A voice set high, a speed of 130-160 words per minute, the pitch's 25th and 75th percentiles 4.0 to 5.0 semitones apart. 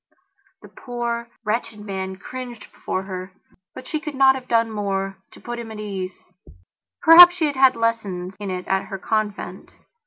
No: high, 220 Hz; average, 175 wpm; average, 4.3 semitones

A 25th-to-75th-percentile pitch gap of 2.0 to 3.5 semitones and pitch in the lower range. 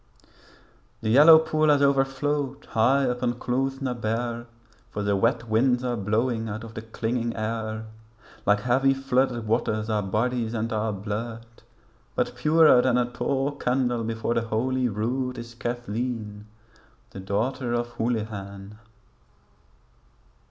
Yes: average, 2.8 semitones; low, 120 Hz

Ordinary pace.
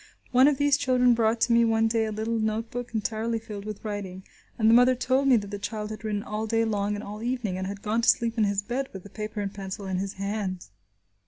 No: fast, 260 wpm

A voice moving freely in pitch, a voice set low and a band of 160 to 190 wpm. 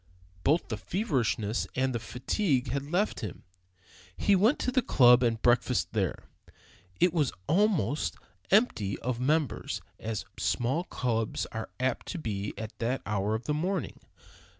No: wide, 6.6 semitones; low, 125 Hz; average, 150 wpm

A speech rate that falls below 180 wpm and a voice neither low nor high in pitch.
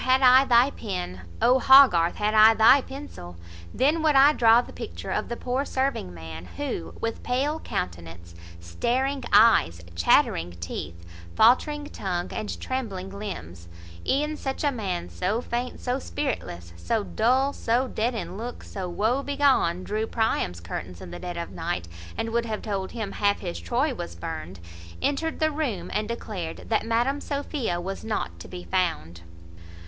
No: average, 165 wpm; high, 220 Hz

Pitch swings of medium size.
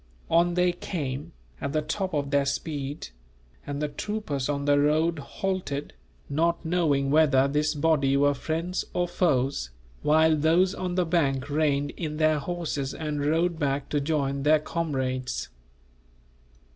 Yes: average, 3.0 semitones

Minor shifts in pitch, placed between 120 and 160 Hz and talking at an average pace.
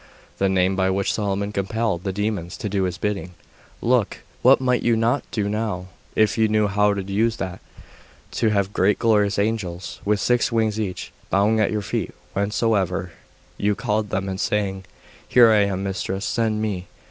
No: narrow, 2.3 semitones; low, 105 Hz; average, 180 wpm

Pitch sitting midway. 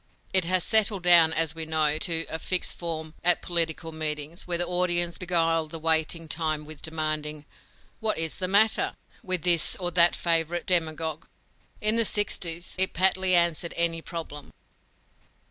Yes: medium, 165 Hz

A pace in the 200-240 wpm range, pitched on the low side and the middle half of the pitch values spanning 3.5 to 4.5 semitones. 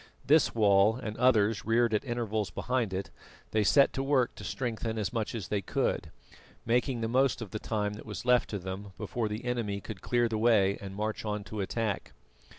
No: fast, 205 wpm; low, 110 Hz; average, 2.7 semitones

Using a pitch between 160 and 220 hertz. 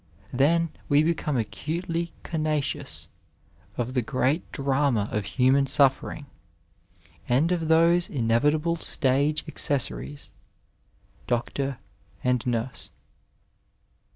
No: medium, 140 Hz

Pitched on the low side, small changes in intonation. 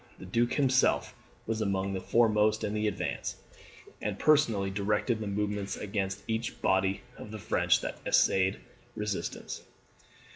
Yes: low, 105 Hz; narrow, 2.2 semitones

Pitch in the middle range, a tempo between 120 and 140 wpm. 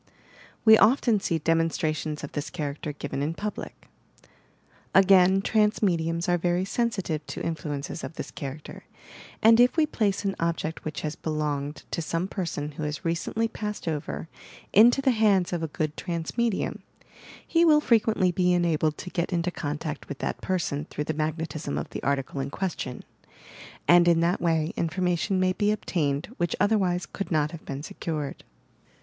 No: medium, 170 Hz; average, 165 wpm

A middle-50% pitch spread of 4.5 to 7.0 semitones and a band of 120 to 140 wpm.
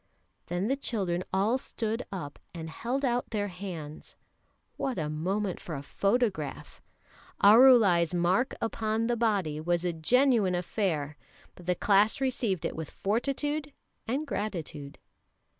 Yes: wide, 5.6 semitones; slow, 135 wpm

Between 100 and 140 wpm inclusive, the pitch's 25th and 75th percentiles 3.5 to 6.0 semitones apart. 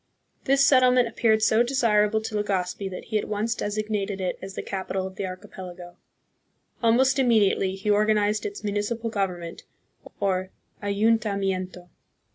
No: slow, 135 wpm; average, 2.8 semitones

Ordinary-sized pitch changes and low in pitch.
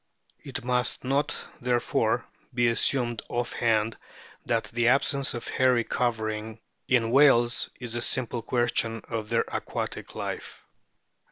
No: narrow, 1.7 semitones; low, 120 Hz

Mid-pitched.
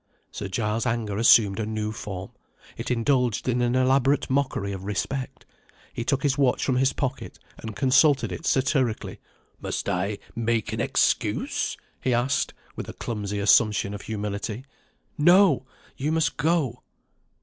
No: low, 120 Hz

